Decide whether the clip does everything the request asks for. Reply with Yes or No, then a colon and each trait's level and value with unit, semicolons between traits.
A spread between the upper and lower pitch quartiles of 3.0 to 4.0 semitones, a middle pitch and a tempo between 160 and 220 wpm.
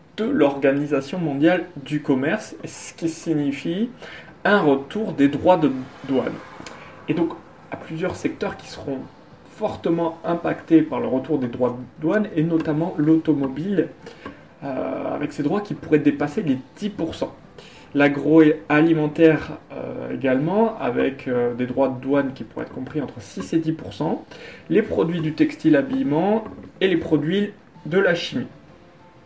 No: average, 3.3 semitones; medium, 155 Hz; slow, 145 wpm